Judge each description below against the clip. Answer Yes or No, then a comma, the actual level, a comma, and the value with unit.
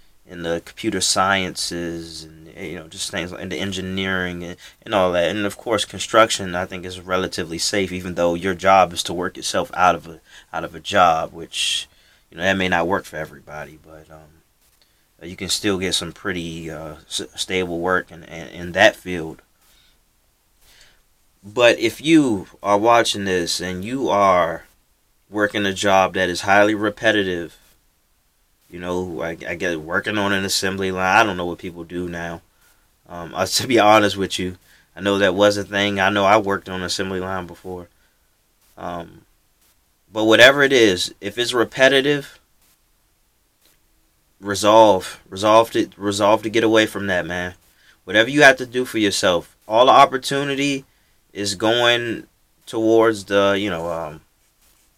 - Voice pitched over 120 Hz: No, very low, 95 Hz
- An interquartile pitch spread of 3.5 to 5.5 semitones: No, average, 3.0 semitones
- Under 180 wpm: Yes, average, 170 wpm